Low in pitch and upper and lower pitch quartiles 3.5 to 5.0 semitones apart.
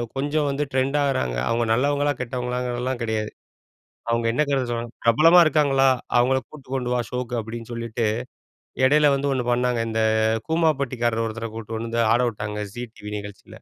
No: low, 125 Hz; average, 3.1 semitones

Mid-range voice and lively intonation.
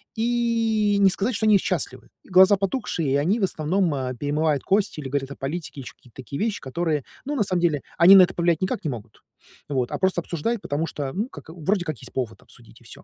Yes: medium, 175 Hz; wide, 5.8 semitones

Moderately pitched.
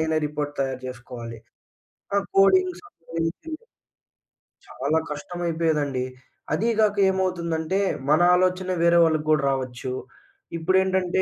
Yes: medium, 165 Hz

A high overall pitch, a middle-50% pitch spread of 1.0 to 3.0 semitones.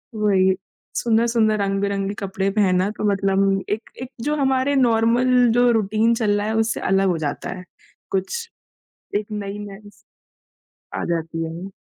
Yes: high, 205 Hz; average, 2.7 semitones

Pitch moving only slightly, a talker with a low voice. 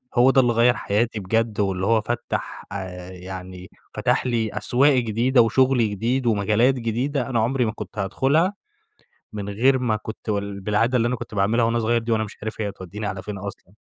No: average, 3.2 semitones; low, 110 Hz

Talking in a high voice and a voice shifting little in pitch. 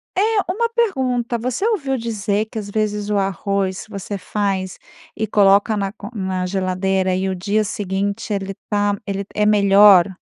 Yes: high, 205 Hz; narrow, 2.2 semitones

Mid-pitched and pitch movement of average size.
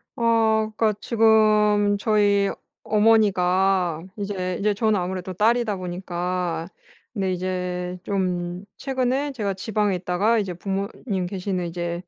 No: high, 195 Hz; average, 3.0 semitones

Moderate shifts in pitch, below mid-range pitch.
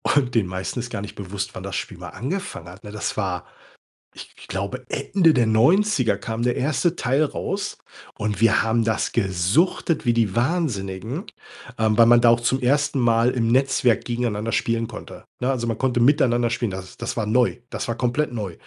Yes: average, 3.6 semitones; low, 120 Hz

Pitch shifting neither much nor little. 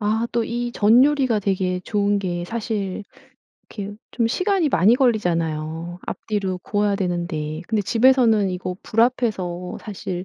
Yes: average, 4.2 semitones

